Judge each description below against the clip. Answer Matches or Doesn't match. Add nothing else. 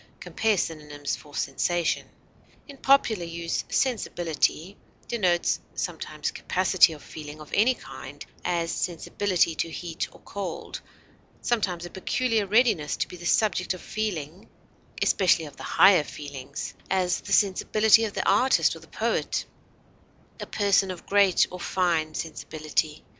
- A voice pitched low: Doesn't match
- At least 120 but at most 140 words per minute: Matches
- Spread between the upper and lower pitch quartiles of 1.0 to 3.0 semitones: Doesn't match